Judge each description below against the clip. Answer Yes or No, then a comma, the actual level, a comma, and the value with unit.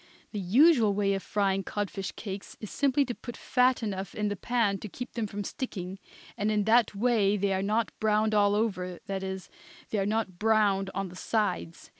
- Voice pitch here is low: No, high, 205 Hz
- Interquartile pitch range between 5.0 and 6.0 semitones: No, narrow, 2.4 semitones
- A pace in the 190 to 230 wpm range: Yes, average, 200 wpm